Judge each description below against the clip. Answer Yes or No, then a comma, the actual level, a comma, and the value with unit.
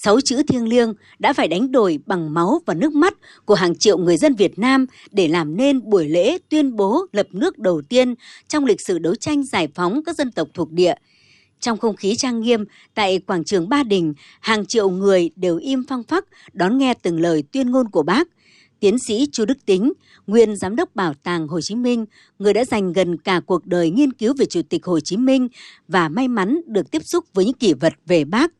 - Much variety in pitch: Yes, wide, 6.6 semitones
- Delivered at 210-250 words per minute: Yes, average, 225 wpm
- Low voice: No, high, 225 Hz